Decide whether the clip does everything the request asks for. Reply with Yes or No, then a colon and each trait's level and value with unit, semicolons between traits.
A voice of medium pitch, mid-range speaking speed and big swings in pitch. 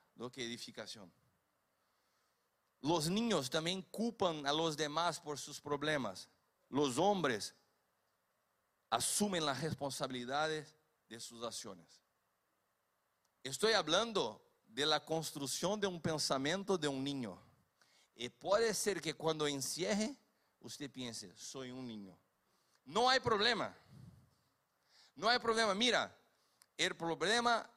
No: medium, 155 Hz; slow, 110 wpm; wide, 5.8 semitones